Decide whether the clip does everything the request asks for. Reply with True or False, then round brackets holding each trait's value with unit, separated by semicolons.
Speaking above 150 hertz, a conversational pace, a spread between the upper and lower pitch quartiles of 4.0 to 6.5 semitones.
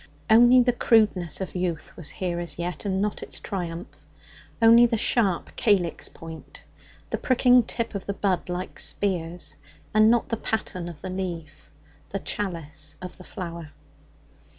True (185 Hz; 155 wpm; 4.3 semitones)